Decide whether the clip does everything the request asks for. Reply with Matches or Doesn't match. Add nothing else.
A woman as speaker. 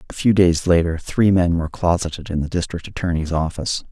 Doesn't match